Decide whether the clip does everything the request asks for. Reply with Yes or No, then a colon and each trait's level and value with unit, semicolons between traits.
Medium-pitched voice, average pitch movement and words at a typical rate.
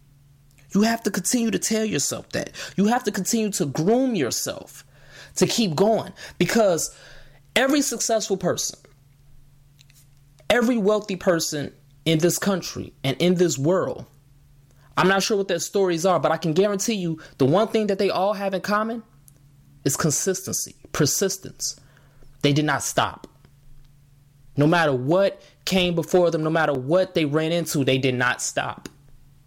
No: medium, 165 Hz; wide, 5.8 semitones; average, 155 wpm